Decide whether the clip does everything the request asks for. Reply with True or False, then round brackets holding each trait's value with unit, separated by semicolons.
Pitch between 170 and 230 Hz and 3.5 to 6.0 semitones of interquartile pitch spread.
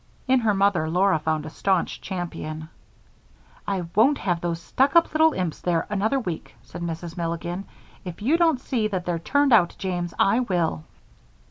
True (185 Hz; 5.0 semitones)